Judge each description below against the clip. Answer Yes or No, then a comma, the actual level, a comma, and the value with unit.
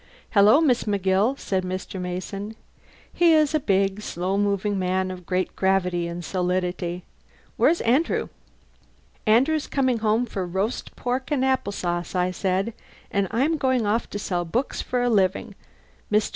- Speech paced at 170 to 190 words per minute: No, average, 155 wpm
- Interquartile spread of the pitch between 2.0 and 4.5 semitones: No, average, 5.0 semitones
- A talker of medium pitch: No, high, 200 Hz